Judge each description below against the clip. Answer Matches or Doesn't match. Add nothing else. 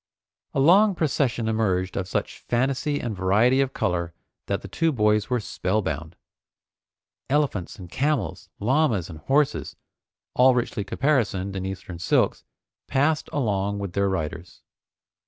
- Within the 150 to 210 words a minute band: Doesn't match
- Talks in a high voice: Doesn't match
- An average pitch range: Doesn't match